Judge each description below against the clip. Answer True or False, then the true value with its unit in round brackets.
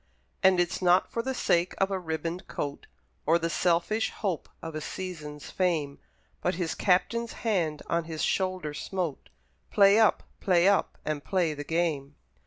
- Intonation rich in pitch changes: False (3.1 semitones)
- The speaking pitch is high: False (175 Hz)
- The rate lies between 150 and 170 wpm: True (165 wpm)